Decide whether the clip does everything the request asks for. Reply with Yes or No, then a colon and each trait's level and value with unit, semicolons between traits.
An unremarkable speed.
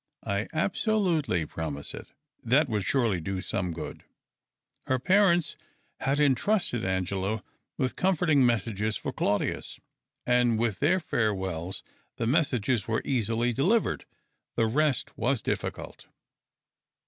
No: slow, 115 wpm